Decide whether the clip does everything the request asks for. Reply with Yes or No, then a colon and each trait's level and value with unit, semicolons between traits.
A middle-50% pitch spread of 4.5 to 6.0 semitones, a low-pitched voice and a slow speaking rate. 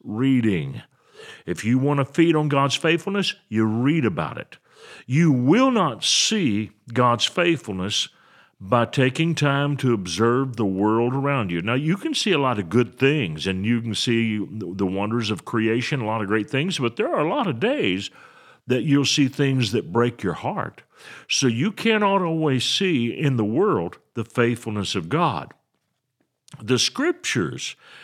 No: average, 5.2 semitones; low, 125 Hz; average, 170 wpm